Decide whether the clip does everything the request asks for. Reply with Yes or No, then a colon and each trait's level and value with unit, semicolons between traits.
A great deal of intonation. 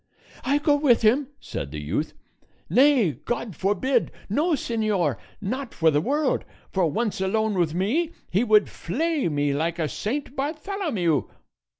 Yes: wide, 8.6 semitones